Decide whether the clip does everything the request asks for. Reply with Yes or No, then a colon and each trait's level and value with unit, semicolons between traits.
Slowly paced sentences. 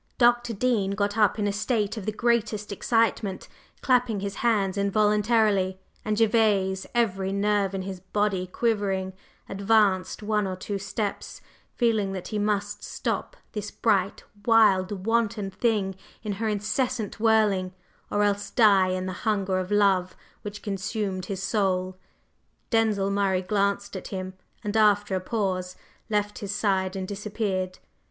No: average, 145 wpm